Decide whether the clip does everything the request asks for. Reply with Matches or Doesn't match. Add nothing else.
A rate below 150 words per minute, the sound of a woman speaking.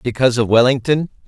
Doesn't match